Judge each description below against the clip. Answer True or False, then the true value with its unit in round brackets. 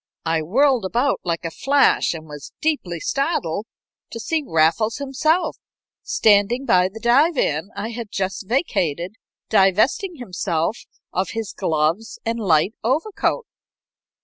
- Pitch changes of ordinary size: False (7.7 semitones)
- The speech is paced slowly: True (125 wpm)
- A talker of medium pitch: False (215 Hz)